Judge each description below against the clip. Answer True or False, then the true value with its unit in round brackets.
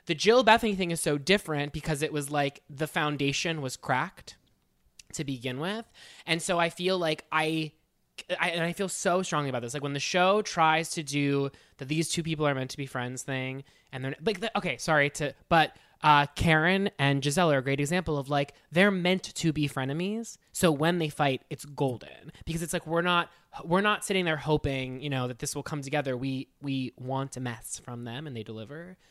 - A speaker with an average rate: False (215 wpm)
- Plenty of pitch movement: False (3.8 semitones)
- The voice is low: False (150 Hz)